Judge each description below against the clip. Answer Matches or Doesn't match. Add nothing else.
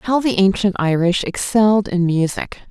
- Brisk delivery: Doesn't match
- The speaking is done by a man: Doesn't match